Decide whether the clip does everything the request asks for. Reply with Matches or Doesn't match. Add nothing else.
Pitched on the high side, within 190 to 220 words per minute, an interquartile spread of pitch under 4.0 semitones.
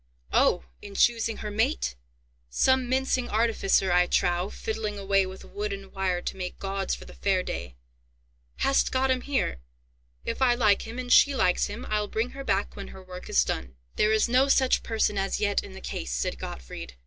Doesn't match